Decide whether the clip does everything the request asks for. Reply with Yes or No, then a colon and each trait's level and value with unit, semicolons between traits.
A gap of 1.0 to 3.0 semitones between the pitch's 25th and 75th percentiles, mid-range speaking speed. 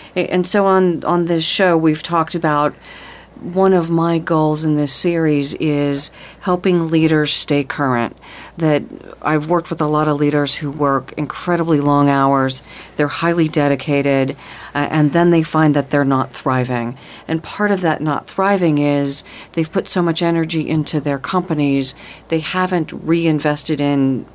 Yes: average, 2.7 semitones; average, 160 wpm